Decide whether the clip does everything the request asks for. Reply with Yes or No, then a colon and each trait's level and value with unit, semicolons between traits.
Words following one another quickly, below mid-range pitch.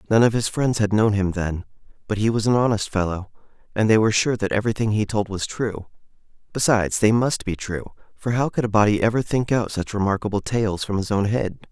Yes: fast, 225 wpm; low, 105 Hz